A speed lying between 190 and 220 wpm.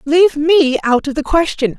Yes: average, 200 wpm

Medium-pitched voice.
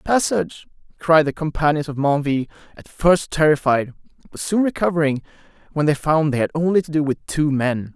Yes: medium, 155 Hz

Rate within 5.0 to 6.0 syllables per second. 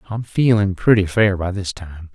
No: 4.7 syllables/s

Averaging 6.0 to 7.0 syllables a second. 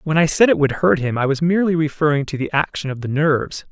Yes: 6.4 syllables/s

